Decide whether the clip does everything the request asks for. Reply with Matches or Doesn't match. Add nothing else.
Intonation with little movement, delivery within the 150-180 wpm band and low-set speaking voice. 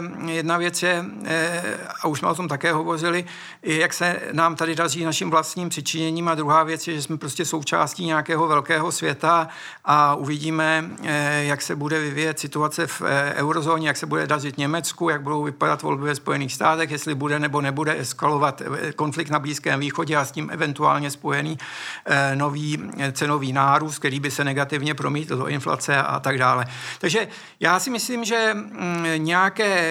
Doesn't match